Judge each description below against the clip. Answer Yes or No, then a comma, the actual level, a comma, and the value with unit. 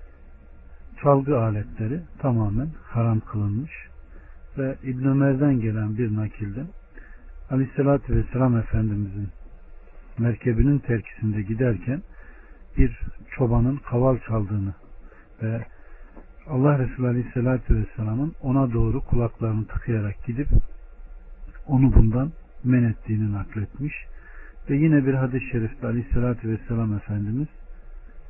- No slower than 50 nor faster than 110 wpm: Yes, slow, 95 wpm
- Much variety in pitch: No, average, 3.9 semitones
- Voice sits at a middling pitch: No, low, 115 Hz